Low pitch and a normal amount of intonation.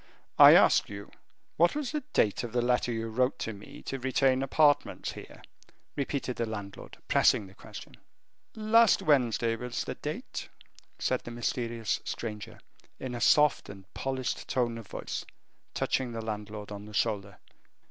Yes: low, 120 Hz; average, 3.6 semitones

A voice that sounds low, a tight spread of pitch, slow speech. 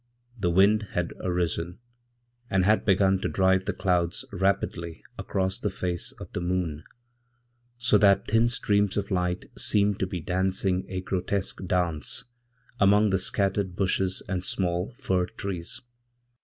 Yes: very low, 95 Hz; narrow, 1.8 semitones; slow, 130 wpm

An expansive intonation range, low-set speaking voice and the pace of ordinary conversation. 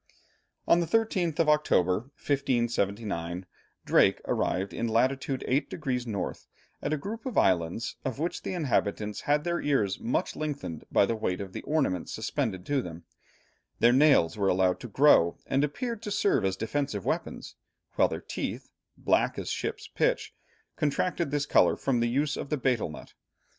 Yes: wide, 7.0 semitones; low, 125 Hz; average, 170 wpm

